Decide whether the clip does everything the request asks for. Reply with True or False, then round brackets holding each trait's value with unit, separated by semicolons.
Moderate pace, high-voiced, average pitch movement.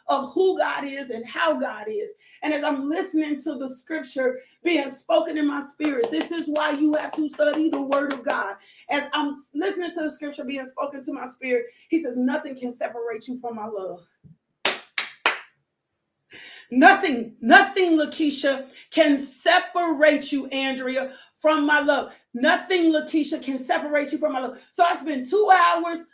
True (170 wpm; 295 Hz; 3.3 semitones)